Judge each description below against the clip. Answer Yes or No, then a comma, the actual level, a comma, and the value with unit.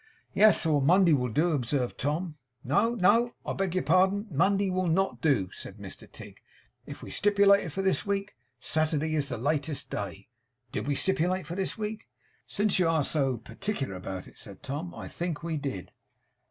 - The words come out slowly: No, average, 180 wpm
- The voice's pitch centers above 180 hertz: No, medium, 165 Hz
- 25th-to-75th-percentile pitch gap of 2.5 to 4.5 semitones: No, average, 5.3 semitones